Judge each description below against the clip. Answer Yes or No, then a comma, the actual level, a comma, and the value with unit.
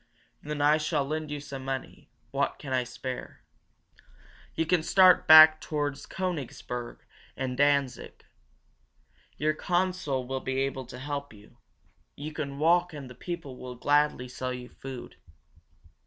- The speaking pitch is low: No, medium, 145 Hz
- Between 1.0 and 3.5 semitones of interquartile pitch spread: Yes, average, 3.1 semitones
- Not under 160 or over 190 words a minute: No, average, 140 wpm